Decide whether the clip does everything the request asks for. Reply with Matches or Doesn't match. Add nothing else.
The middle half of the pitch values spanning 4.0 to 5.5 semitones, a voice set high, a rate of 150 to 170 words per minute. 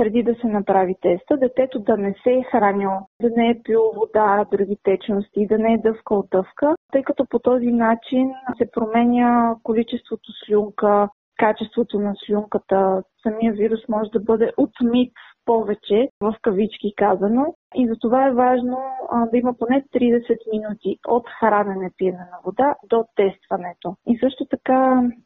Doesn't match